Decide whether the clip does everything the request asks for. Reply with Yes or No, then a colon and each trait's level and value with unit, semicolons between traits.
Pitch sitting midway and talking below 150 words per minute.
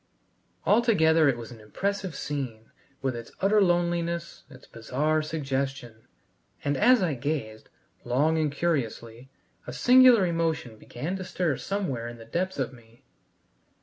Yes: medium, 150 Hz; slow, 135 wpm